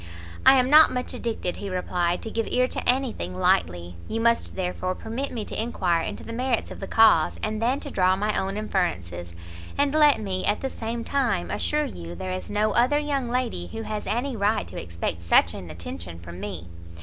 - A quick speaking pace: Yes, fast, 210 wpm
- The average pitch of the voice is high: Yes, high, 215 Hz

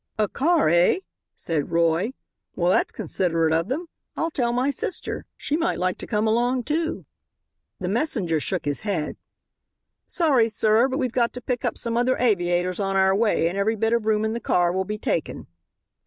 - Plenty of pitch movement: Yes, wide, 5.7 semitones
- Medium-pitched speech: No, high, 215 Hz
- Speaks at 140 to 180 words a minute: No, average, 190 wpm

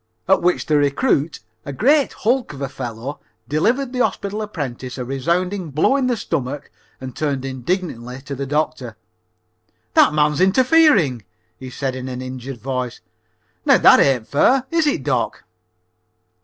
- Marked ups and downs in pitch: Yes, wide, 7.4 semitones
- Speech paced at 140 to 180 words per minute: Yes, average, 155 wpm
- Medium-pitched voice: Yes, medium, 145 Hz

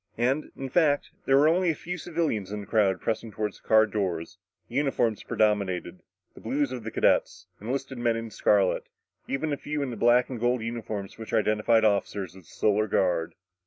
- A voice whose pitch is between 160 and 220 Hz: No, low, 115 Hz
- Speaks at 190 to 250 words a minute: Yes, average, 200 wpm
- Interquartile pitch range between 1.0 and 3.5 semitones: No, average, 4.5 semitones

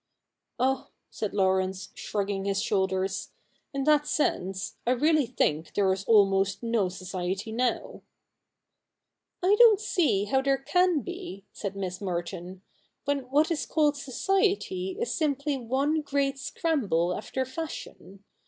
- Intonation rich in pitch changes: Yes, wide, 7.5 semitones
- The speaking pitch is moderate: No, high, 245 Hz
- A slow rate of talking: No, average, 145 wpm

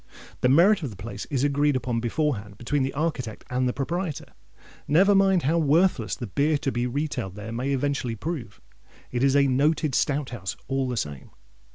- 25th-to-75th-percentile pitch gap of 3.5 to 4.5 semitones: Yes, average, 3.9 semitones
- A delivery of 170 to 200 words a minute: Yes, average, 190 wpm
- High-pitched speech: No, low, 135 Hz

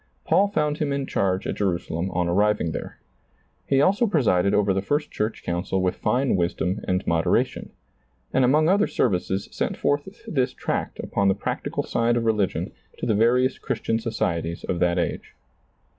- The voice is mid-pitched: No, low, 105 Hz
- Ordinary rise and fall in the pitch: No, wide, 6.5 semitones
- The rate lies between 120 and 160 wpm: No, average, 175 wpm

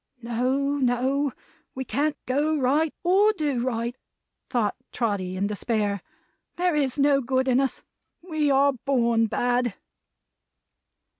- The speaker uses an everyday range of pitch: Yes, average, 3.4 semitones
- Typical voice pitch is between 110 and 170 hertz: No, very high, 260 Hz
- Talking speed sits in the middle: No, slow, 125 wpm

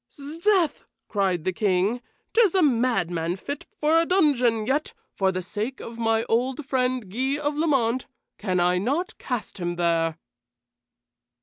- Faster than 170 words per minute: No, average, 150 wpm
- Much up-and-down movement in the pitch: Yes, wide, 7.5 semitones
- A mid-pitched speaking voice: No, high, 240 Hz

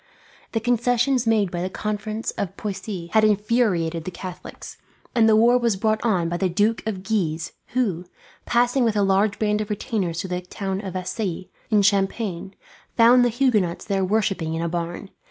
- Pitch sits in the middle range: No, high, 205 Hz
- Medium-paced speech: Yes, average, 180 wpm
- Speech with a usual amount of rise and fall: Yes, average, 3.6 semitones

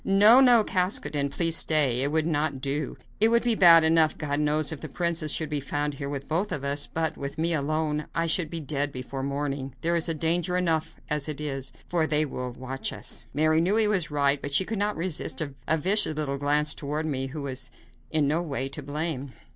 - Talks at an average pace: No, fast, 220 wpm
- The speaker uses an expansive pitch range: No, average, 2.9 semitones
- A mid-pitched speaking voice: Yes, medium, 155 Hz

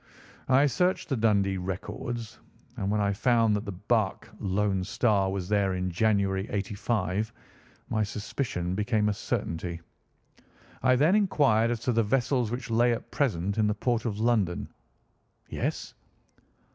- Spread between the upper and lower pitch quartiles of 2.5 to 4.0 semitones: Yes, average, 3.5 semitones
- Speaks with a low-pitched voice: Yes, low, 105 Hz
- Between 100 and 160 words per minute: Yes, average, 145 wpm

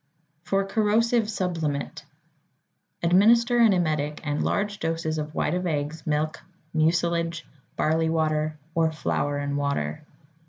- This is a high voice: No, medium, 160 Hz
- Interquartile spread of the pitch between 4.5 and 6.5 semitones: No, average, 3.7 semitones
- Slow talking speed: Yes, slow, 120 wpm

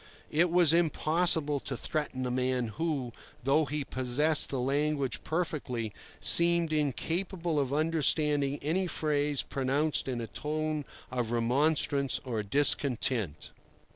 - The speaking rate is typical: No, slow, 120 wpm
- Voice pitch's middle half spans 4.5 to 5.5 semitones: No, average, 3.4 semitones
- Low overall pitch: No, medium, 145 Hz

